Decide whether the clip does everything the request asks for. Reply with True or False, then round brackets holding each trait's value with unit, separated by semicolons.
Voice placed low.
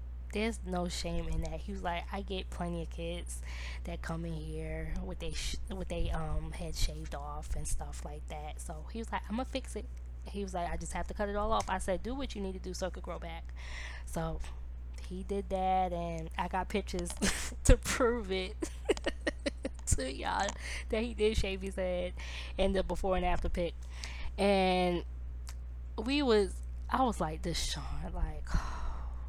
False (170 Hz)